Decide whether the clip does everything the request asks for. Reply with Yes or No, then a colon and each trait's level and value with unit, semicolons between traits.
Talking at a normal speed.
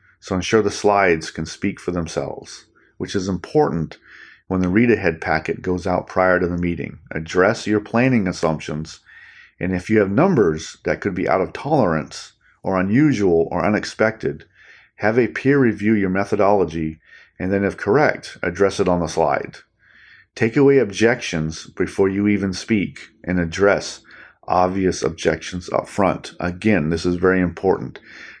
Yes: average, 155 wpm